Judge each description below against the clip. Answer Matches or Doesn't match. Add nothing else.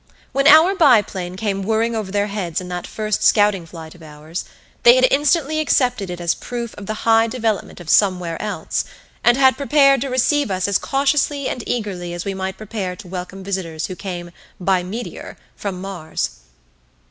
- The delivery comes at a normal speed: Matches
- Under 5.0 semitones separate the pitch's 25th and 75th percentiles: Doesn't match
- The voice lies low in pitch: Doesn't match